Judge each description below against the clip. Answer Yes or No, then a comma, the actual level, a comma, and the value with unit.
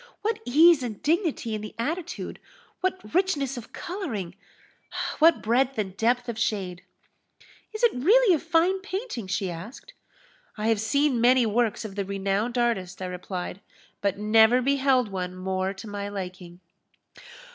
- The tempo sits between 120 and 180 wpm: Yes, average, 150 wpm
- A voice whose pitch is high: Yes, high, 230 Hz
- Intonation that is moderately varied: No, wide, 7.0 semitones